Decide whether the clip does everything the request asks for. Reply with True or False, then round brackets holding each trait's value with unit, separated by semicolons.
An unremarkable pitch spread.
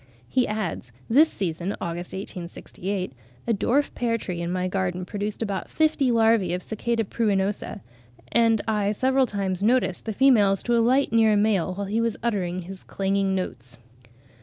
True (3.8 semitones)